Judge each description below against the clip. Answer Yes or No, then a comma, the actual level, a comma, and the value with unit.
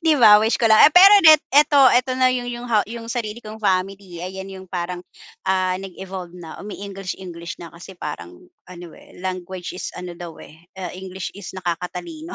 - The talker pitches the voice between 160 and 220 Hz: Yes, high, 190 Hz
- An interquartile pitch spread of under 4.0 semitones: No, average, 4.4 semitones